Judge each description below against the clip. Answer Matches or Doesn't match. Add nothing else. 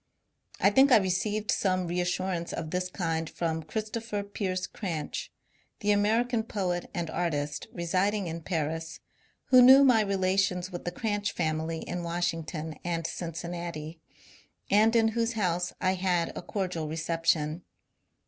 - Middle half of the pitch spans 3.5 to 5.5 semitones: Matches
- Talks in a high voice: Doesn't match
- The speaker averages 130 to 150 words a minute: Matches